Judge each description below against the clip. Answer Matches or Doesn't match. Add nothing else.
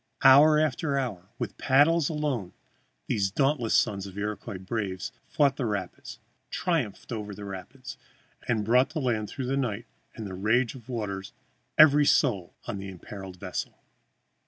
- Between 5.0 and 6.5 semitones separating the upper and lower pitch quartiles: Matches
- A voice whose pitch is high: Doesn't match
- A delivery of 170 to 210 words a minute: Doesn't match